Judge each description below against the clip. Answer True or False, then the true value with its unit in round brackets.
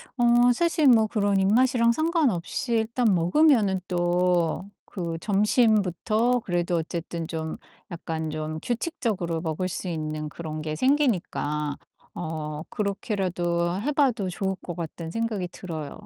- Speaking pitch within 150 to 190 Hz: True (185 Hz)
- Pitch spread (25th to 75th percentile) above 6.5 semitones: False (5.8 semitones)